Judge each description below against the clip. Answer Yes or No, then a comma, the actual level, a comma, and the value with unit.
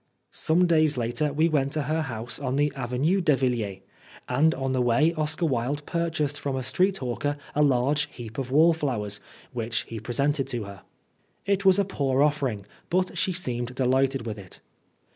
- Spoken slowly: No, average, 180 wpm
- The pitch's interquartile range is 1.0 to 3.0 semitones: No, average, 4.2 semitones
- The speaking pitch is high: No, medium, 140 Hz